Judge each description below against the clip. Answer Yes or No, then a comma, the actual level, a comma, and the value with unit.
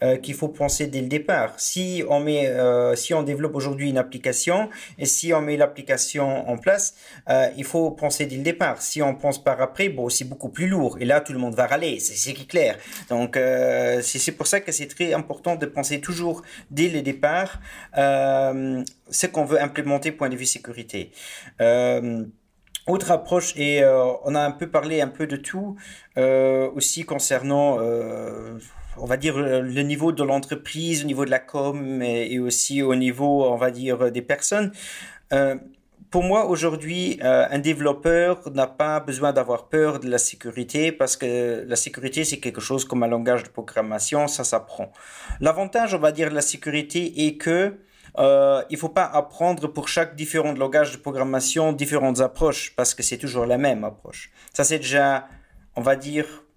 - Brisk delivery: No, average, 190 wpm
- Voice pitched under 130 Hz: No, medium, 140 Hz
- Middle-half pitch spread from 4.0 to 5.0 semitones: No, average, 3.4 semitones